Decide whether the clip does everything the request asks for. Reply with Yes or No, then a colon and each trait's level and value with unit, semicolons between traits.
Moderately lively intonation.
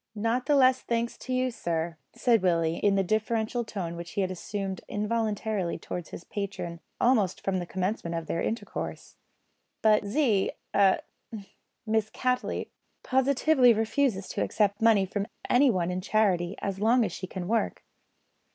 Yes: average, 3.9 semitones